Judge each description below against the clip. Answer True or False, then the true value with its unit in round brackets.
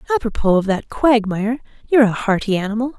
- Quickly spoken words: False (160 wpm)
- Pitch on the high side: True (225 Hz)